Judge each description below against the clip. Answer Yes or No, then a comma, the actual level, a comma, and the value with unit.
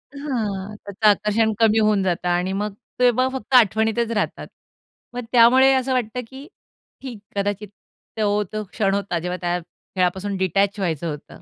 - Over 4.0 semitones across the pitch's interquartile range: No, average, 3.4 semitones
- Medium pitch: No, high, 210 Hz